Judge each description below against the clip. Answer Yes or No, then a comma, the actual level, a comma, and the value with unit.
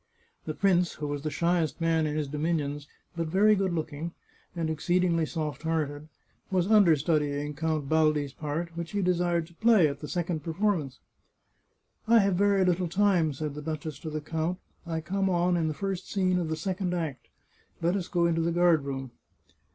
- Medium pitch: Yes, medium, 165 Hz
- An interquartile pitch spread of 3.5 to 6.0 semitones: No, average, 2.9 semitones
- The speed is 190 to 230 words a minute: Yes, average, 195 wpm